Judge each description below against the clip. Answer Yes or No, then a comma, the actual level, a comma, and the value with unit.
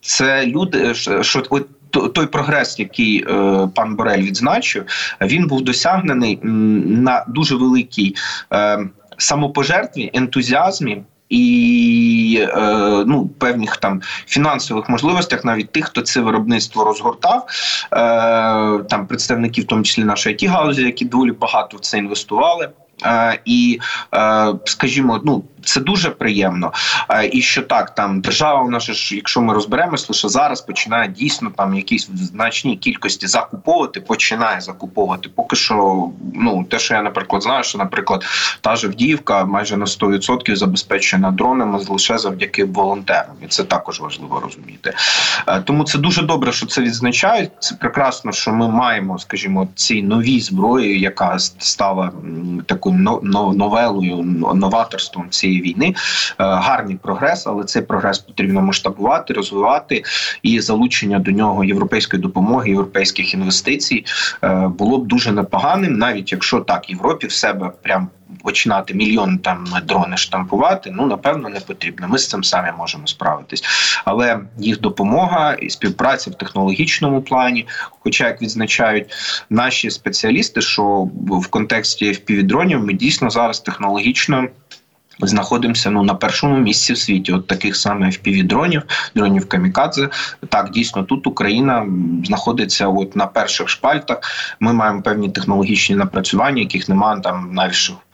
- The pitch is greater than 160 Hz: No, low, 110 Hz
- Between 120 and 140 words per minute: Yes, average, 130 wpm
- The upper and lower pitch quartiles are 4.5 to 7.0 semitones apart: Yes, average, 4.9 semitones